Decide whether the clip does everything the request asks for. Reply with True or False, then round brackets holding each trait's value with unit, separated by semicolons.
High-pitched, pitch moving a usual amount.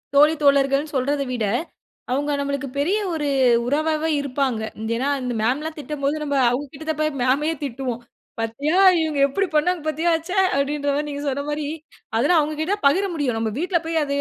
False (285 Hz; 2.2 semitones)